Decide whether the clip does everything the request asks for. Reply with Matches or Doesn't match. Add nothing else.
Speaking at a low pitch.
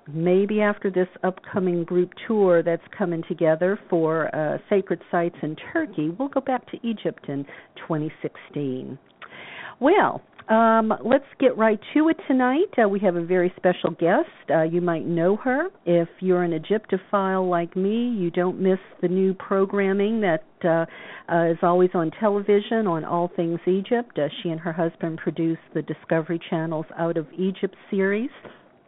Doesn't match